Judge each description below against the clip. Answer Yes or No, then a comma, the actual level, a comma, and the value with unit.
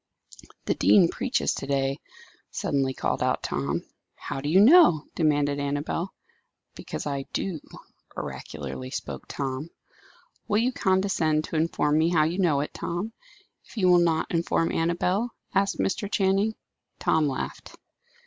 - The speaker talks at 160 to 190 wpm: No, average, 140 wpm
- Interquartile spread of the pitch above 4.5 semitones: Yes, average, 5.1 semitones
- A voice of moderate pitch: Yes, medium, 165 Hz